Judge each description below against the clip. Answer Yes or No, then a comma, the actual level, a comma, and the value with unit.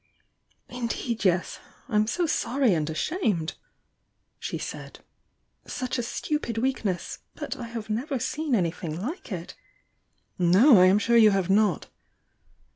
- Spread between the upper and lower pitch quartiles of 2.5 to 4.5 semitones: No, average, 5.3 semitones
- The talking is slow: Yes, slow, 130 wpm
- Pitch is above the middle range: Yes, high, 225 Hz